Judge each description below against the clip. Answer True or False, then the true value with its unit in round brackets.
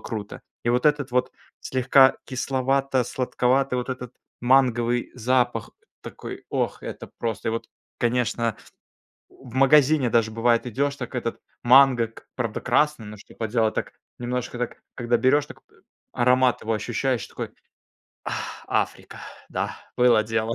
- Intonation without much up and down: True (2.1 semitones)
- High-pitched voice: False (125 Hz)